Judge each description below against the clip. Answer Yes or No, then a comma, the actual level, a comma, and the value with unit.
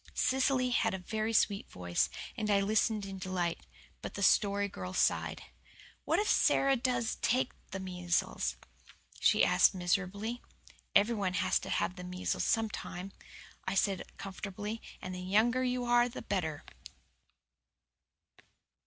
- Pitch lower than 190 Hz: No, high, 200 Hz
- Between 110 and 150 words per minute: Yes, slow, 135 wpm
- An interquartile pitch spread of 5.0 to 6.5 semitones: No, average, 3.7 semitones